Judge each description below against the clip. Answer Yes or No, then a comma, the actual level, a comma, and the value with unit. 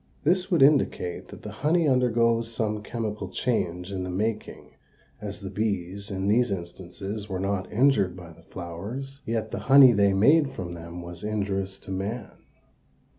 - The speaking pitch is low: Yes, low, 105 Hz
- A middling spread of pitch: Yes, average, 4.1 semitones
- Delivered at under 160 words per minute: No, average, 165 wpm